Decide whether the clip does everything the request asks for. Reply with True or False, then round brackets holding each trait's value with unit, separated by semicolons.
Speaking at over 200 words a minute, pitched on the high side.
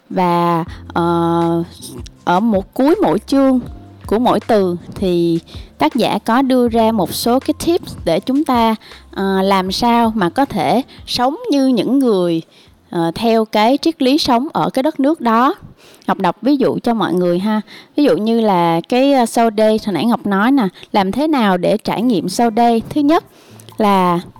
False (185 wpm; 225 Hz)